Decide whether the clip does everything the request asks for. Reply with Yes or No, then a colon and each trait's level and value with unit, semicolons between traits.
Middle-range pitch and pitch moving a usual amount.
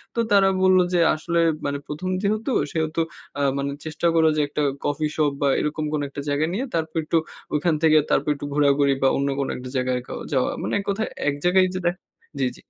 Yes: medium, 155 Hz; average, 3.8 semitones